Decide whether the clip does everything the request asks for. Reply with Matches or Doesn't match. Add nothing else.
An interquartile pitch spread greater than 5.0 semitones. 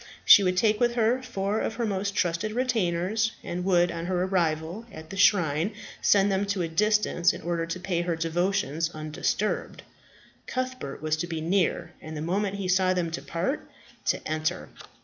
Doesn't match